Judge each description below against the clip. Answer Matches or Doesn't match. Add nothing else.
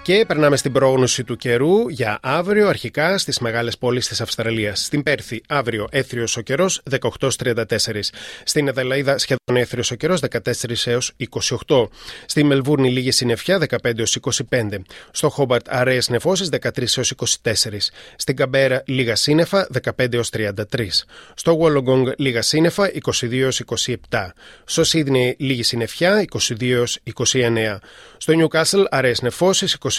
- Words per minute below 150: Matches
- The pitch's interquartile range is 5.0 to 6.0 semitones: Doesn't match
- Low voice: Matches